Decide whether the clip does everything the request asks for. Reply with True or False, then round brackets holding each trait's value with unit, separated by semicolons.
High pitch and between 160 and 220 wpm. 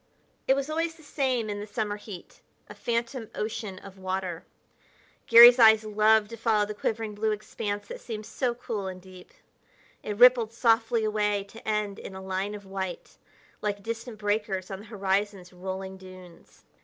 True (210 Hz; 170 wpm)